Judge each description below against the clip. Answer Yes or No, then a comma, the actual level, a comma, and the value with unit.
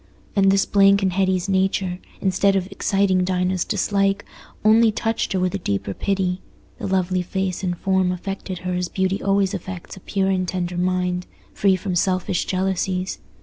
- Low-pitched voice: No, high, 190 Hz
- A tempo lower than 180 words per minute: Yes, average, 170 wpm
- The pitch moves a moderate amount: No, narrow, 1.3 semitones